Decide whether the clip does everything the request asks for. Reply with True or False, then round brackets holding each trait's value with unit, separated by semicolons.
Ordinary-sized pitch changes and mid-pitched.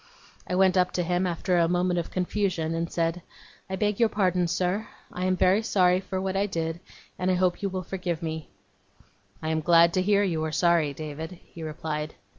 False (2.2 semitones; 180 Hz)